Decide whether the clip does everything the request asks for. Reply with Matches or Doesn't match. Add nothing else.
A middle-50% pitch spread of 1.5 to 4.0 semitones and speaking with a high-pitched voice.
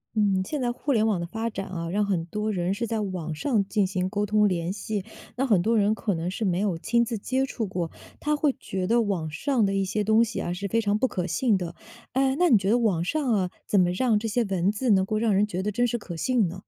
Matches